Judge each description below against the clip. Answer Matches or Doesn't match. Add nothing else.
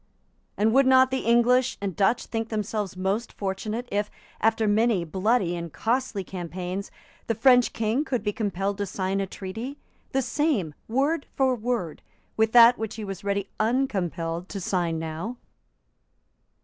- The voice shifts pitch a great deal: Doesn't match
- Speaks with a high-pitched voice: Matches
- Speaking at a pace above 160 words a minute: Doesn't match